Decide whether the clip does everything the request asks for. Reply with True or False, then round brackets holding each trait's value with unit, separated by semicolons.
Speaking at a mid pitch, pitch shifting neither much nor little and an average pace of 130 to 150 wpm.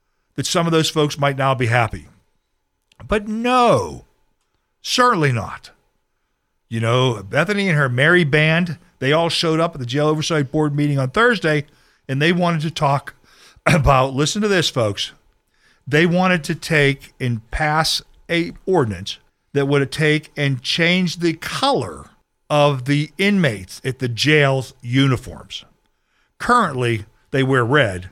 True (150 Hz; 4.0 semitones; 145 wpm)